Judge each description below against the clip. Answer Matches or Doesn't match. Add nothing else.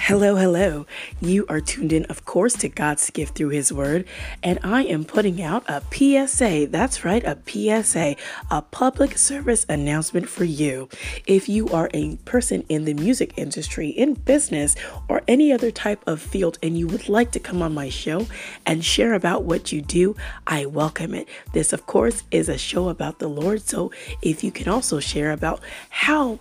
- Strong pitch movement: Matches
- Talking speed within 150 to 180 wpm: Doesn't match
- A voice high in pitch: Doesn't match